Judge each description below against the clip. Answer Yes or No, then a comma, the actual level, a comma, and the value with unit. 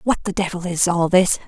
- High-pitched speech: No, medium, 180 Hz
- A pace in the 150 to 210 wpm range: No, fast, 245 wpm